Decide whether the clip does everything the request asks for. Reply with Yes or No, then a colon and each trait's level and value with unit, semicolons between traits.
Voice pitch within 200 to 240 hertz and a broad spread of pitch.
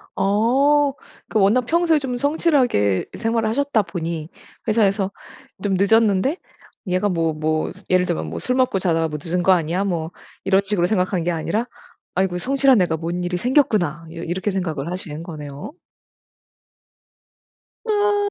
No: high, 190 Hz; wide, 6.5 semitones